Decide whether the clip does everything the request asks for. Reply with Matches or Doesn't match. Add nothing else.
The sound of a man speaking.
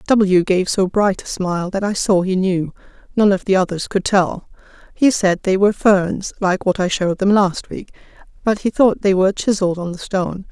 Doesn't match